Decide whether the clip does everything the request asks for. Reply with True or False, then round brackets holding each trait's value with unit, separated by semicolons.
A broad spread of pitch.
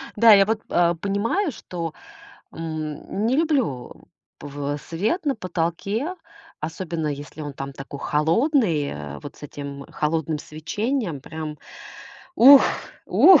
True (7.0 semitones)